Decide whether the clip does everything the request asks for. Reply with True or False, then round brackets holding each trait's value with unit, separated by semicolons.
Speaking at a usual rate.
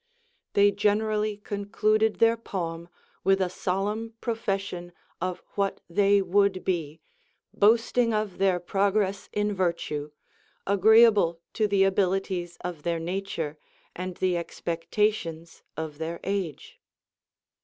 False (110 wpm)